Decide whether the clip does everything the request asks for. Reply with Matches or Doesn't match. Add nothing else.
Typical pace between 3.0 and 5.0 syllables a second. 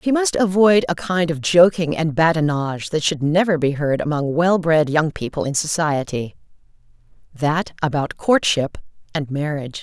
Matches